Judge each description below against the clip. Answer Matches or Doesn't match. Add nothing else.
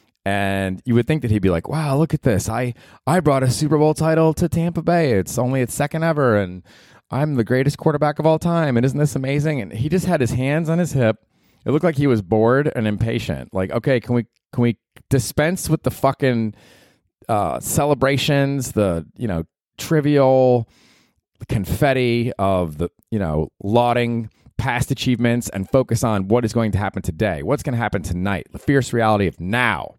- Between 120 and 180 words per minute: Doesn't match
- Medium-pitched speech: Doesn't match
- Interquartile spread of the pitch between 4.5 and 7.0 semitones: Matches